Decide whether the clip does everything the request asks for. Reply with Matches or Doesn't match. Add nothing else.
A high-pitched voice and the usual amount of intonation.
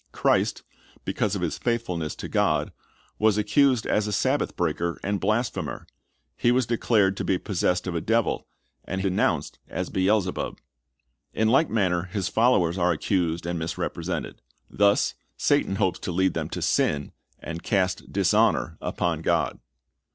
Doesn't match